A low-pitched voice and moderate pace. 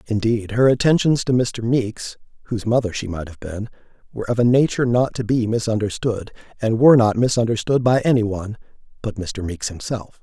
Yes: low, 115 Hz; average, 175 wpm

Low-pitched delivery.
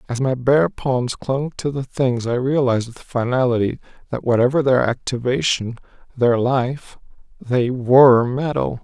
Yes: low, 130 Hz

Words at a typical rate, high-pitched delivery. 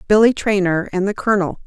Yes: average, 180 wpm; high, 195 Hz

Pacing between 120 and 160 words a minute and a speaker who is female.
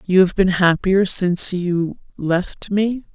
Yes: slow, 135 wpm; female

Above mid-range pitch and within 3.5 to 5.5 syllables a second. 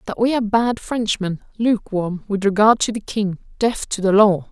Yes: high, 210 Hz; 5.0 syllables/s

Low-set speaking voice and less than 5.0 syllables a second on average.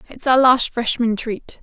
No: high, 240 Hz; 4.2 syllables/s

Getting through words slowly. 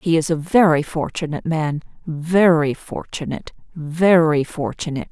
Yes: slow, 95 wpm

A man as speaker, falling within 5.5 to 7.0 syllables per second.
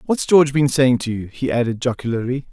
Yes: male; 6.0 syllables/s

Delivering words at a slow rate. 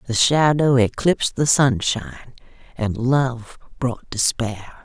Yes: slow, 110 wpm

